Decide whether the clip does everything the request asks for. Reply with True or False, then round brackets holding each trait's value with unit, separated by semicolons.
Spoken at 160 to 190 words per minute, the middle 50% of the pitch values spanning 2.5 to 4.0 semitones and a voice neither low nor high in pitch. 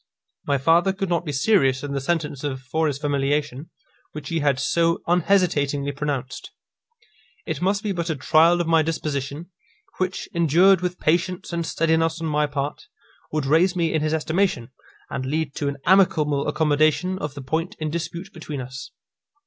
True (170 wpm; 3.3 semitones; 155 Hz)